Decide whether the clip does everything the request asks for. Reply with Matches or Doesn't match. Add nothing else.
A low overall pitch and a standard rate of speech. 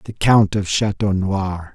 Matches